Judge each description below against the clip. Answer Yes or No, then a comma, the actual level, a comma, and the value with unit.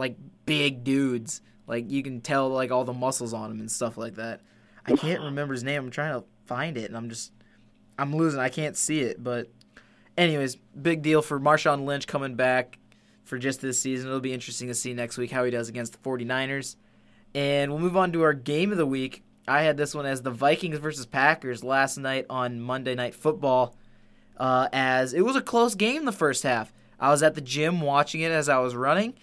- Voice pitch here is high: No, low, 135 Hz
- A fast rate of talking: Yes, fast, 220 wpm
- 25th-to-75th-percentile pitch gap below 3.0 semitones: No, average, 3.3 semitones